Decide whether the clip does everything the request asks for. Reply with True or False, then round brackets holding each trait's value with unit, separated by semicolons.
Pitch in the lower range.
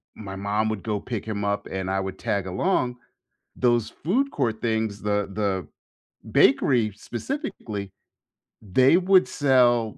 True (110 Hz)